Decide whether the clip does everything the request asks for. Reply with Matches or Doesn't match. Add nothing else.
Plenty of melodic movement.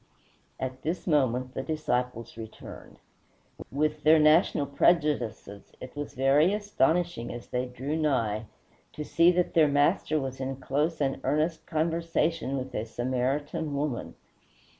Doesn't match